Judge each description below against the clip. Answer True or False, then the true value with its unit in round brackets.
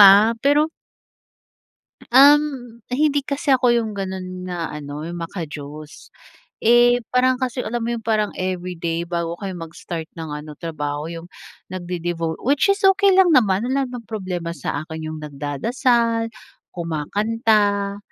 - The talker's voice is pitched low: False (195 Hz)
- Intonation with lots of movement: True (6.7 semitones)